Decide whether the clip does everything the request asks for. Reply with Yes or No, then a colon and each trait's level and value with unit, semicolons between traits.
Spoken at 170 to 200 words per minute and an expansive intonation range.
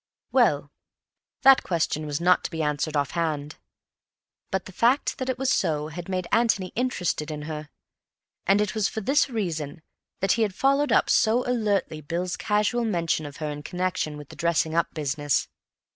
Yes: average, 180 wpm; wide, 6.1 semitones